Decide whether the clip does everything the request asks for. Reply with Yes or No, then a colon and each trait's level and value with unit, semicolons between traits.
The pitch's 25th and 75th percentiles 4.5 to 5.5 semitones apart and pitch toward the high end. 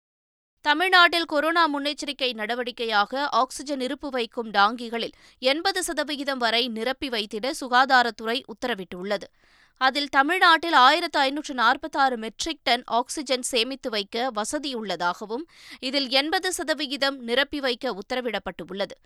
No: average, 4.0 semitones; very high, 260 Hz